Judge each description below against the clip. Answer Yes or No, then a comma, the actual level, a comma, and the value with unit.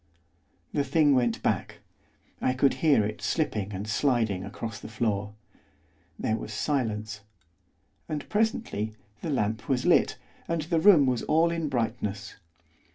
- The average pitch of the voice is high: No, low, 120 Hz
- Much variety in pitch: Yes, wide, 5.8 semitones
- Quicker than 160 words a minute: No, average, 140 wpm